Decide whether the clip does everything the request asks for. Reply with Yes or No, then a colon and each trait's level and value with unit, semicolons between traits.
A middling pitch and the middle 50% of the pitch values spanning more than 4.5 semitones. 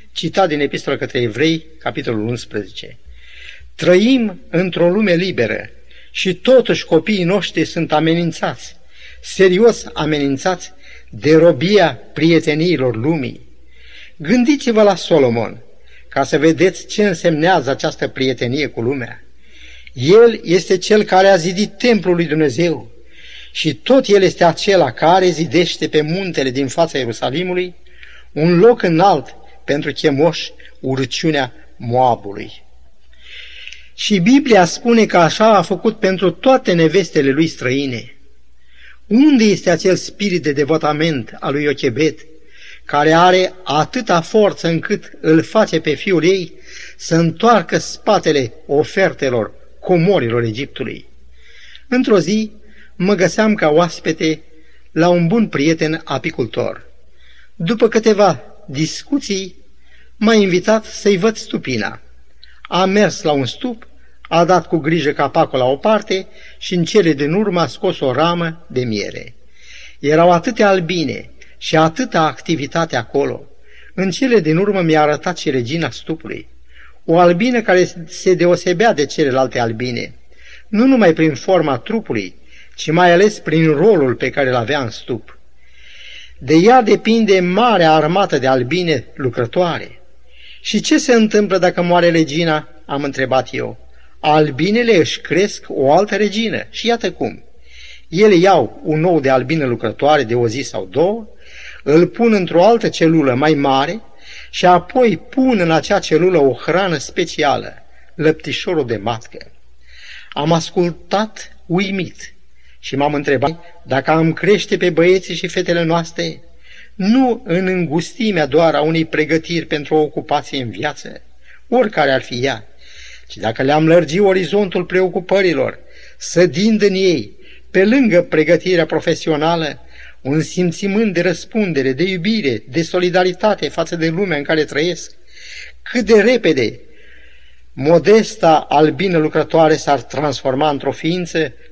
Yes: medium, 165 Hz; average, 5.0 semitones